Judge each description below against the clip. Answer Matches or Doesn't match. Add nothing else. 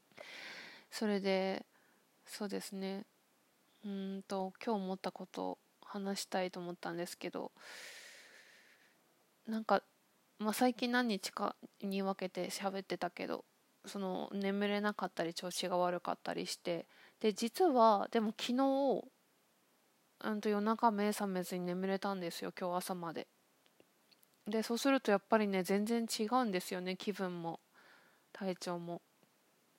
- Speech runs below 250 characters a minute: Doesn't match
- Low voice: Doesn't match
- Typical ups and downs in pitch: Matches